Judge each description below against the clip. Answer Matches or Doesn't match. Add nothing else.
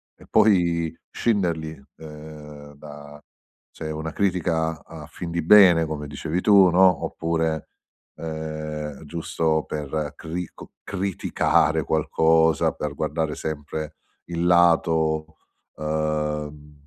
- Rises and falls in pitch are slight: Matches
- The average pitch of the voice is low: Matches